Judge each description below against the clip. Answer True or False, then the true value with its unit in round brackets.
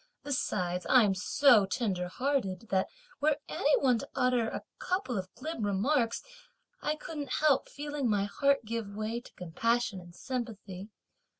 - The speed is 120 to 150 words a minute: True (145 wpm)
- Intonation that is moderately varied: False (5.9 semitones)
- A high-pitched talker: True (230 Hz)